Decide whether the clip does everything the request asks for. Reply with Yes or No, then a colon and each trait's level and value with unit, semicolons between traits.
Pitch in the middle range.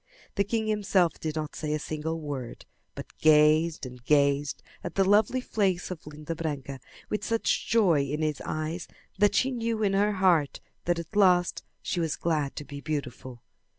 Yes: medium, 160 Hz